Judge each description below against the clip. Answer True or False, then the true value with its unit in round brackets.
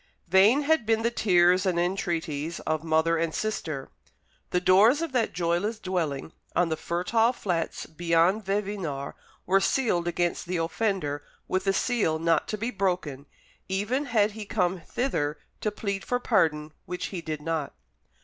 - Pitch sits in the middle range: True (180 Hz)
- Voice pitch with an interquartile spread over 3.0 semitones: True (4.4 semitones)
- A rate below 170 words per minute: True (160 wpm)